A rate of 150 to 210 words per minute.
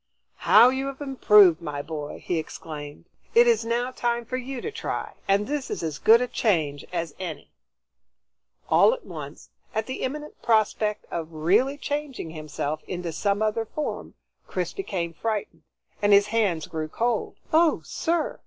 Yes: average, 160 wpm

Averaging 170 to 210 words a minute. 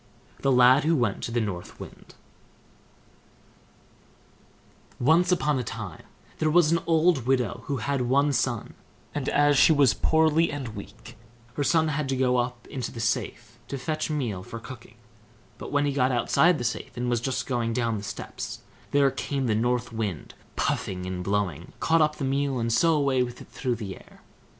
Yes: average, 185 wpm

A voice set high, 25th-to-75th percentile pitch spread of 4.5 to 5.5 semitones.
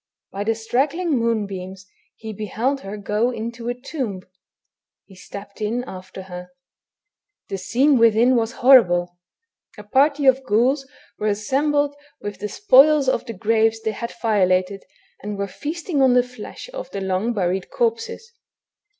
Yes: high, 225 Hz; average, 5.0 semitones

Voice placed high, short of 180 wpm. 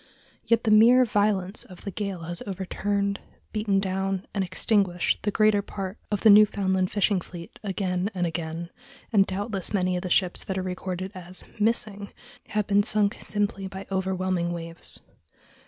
Yes: high, 195 Hz; average, 160 wpm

